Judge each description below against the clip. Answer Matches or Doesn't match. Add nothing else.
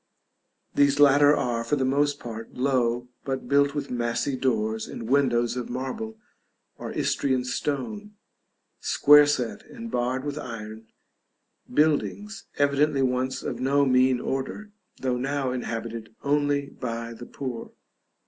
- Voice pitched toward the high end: Doesn't match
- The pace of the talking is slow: Matches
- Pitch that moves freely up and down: Doesn't match